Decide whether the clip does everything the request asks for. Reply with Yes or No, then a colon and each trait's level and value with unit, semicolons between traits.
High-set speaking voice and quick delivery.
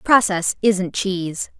No: high, 195 Hz; slow, 115 wpm